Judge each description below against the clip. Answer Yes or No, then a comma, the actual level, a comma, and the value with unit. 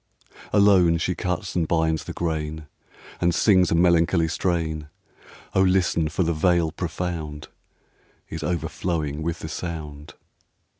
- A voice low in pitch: Yes, very low, 85 Hz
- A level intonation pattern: Yes, narrow, 2.1 semitones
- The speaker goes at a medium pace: No, slow, 130 wpm